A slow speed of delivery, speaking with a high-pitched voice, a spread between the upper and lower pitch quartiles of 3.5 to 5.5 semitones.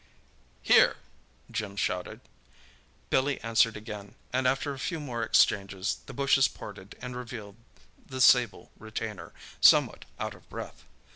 No: slow, 130 wpm; low, 115 Hz; average, 4.3 semitones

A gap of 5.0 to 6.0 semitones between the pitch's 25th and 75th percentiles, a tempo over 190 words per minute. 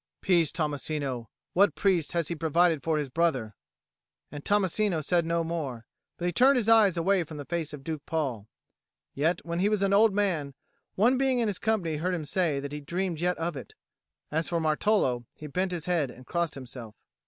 No: average, 4.1 semitones; average, 200 wpm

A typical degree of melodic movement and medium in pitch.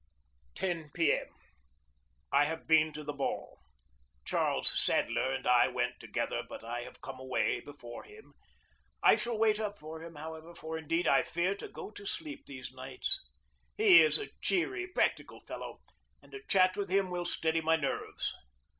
No: wide, 6.2 semitones; medium, 160 Hz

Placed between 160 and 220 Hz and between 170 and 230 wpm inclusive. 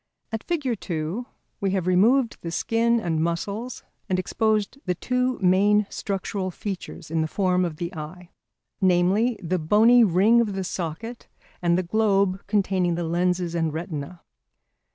No: medium, 185 Hz; average, 155 wpm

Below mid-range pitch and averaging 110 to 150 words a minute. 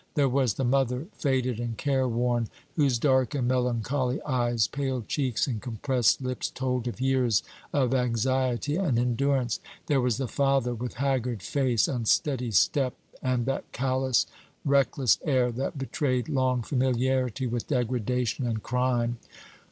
Yes: low, 125 Hz; average, 145 wpm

